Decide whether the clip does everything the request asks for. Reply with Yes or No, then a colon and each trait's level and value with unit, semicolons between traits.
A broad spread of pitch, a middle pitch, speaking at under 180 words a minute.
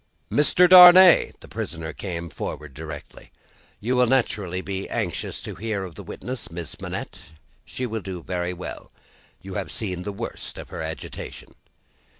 No: wide, 6.0 semitones; very low, 95 Hz; average, 155 wpm